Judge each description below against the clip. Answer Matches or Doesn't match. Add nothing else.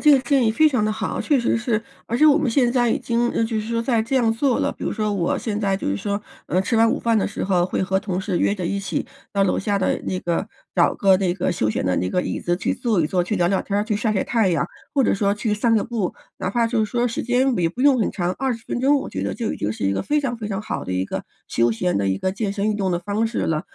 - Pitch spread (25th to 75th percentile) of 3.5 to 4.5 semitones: Matches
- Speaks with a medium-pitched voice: Doesn't match